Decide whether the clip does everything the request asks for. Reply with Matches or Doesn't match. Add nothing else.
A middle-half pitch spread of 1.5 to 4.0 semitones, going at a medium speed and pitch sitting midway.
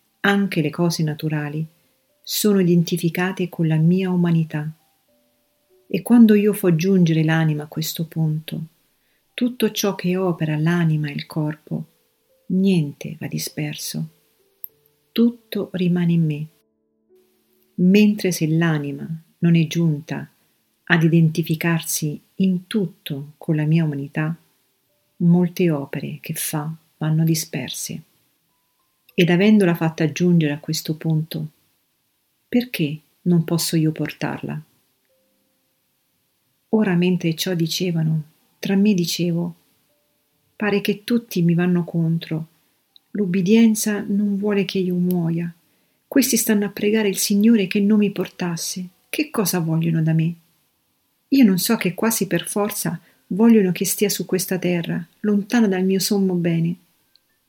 Matches